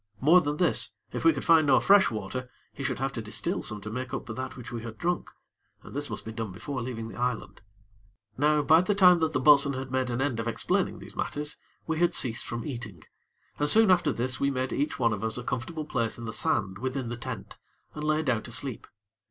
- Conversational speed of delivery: No, fast, 240 wpm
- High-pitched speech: No, low, 130 Hz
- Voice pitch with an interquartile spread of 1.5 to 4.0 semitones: No, average, 4.5 semitones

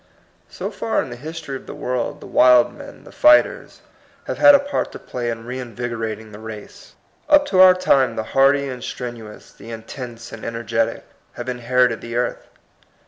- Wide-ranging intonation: No, average, 3.3 semitones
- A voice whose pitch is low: Yes, low, 125 Hz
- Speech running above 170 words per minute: Yes, average, 180 wpm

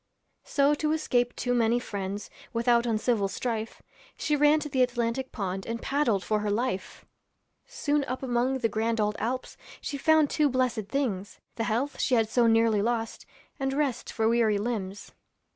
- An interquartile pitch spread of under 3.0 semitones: No, average, 3.3 semitones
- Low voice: No, high, 235 Hz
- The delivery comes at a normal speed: Yes, average, 170 wpm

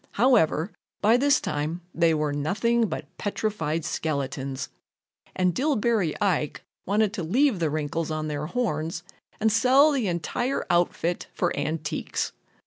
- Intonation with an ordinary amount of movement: No, wide, 6.5 semitones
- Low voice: No, medium, 175 Hz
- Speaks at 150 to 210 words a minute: No, slow, 135 wpm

